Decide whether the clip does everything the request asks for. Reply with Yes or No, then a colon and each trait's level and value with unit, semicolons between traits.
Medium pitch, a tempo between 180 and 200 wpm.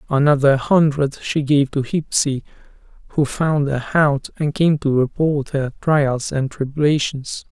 No: medium, 145 Hz; average, 140 wpm